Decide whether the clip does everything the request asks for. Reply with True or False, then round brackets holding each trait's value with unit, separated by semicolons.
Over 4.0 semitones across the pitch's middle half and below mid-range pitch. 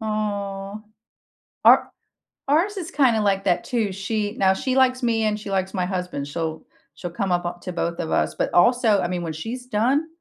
False (4.6 semitones; 205 Hz)